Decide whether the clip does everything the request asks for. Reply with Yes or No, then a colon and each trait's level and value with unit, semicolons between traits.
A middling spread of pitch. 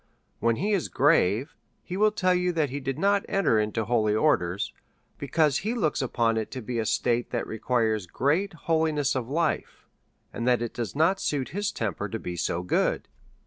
No: wide, 6.7 semitones